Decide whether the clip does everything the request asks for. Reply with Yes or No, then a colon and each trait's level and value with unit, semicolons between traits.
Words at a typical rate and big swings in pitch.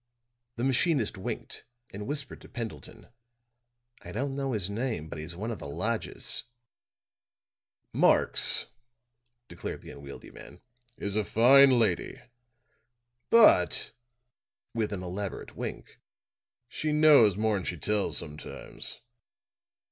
No: slow, 115 wpm; wide, 6.3 semitones